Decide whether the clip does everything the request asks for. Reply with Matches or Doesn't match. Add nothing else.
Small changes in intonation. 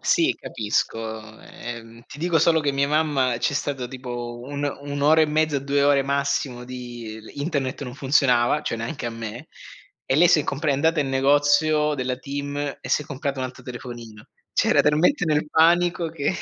Doesn't match